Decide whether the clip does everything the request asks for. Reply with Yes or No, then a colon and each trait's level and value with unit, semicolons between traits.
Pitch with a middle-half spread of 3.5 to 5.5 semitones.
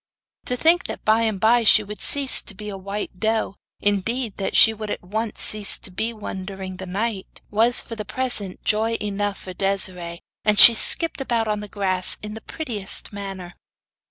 No: narrow, 2.6 semitones